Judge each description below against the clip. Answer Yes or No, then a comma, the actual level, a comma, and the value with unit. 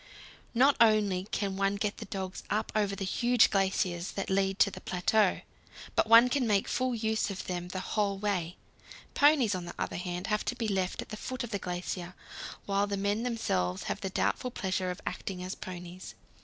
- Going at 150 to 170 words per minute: No, average, 200 wpm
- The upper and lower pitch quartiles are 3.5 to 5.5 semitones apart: No, average, 3.0 semitones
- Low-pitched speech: No, high, 195 Hz